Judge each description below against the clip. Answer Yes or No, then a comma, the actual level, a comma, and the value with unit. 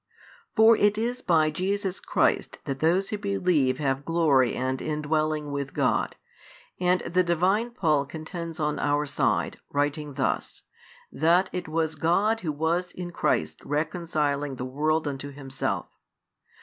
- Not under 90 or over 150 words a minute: Yes, average, 140 wpm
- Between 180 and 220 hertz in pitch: No, medium, 155 Hz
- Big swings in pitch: No, average, 3.9 semitones